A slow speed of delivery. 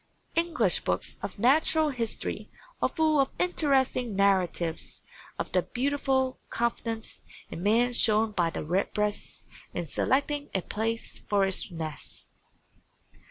Yes: slow, 120 wpm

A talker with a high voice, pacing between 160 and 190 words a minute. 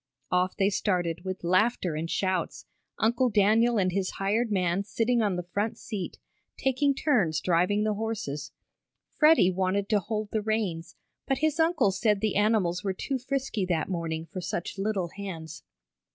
Yes: high, 200 Hz; average, 165 wpm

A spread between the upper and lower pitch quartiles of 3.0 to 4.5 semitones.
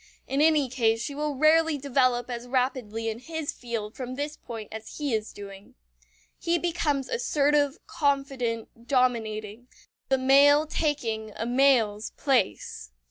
Yes: average, 4.2 semitones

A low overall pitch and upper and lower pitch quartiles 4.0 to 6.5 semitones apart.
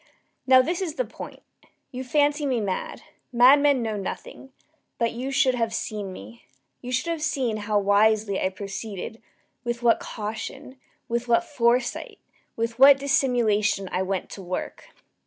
No: high, 235 Hz; average, 4.4 semitones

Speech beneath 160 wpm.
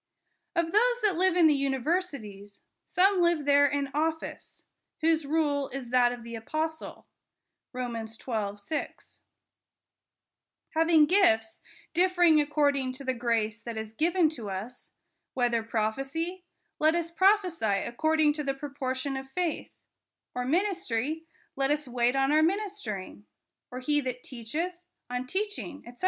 Yes: average, 140 wpm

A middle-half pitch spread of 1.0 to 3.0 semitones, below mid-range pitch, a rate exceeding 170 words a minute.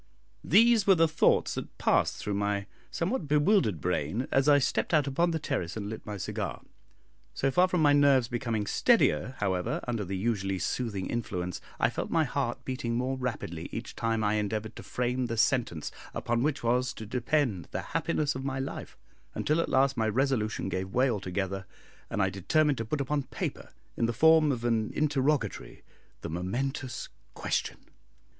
No: wide, 5.5 semitones; low, 120 Hz; average, 180 wpm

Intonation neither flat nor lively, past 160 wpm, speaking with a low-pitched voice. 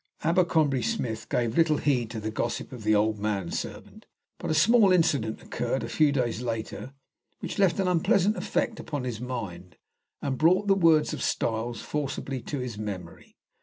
No: wide, 6.5 semitones; average, 175 wpm; low, 125 Hz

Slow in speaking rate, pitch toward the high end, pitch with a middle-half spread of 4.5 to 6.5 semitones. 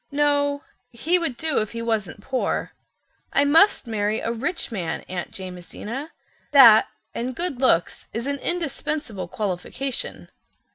Yes: slow, 125 wpm; very high, 250 Hz; average, 5.3 semitones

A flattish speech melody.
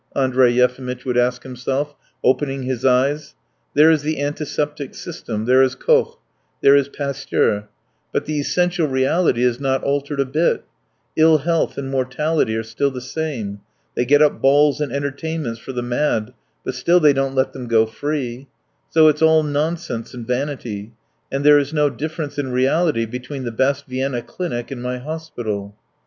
No: average, 3.0 semitones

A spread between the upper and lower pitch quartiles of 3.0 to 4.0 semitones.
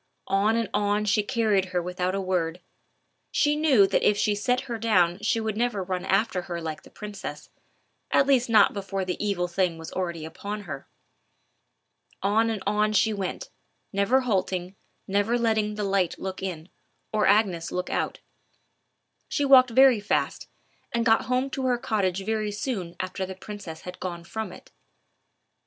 Yes: average, 3.3 semitones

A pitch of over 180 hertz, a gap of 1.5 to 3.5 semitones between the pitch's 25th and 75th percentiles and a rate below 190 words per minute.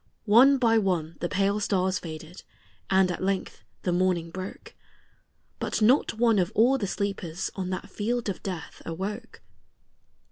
Yes: high, 190 Hz; average, 3.0 semitones; average, 150 wpm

